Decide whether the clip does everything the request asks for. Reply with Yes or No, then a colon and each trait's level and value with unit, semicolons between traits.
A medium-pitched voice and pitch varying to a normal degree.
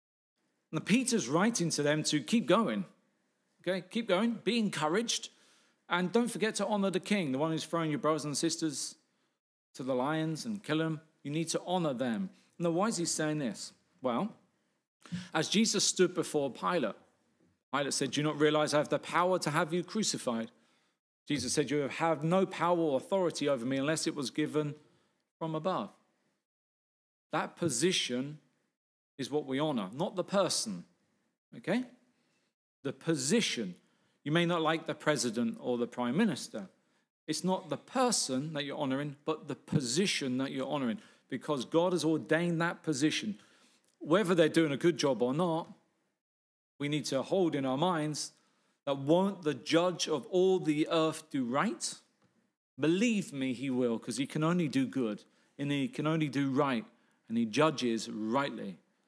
Yes: medium, 160 Hz; average, 4.2 semitones